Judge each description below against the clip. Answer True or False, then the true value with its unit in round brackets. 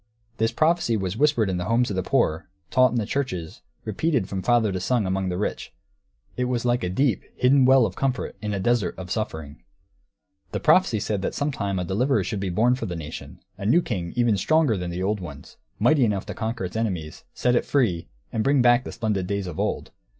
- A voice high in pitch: False (110 Hz)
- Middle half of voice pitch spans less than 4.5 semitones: False (5.0 semitones)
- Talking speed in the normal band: False (225 wpm)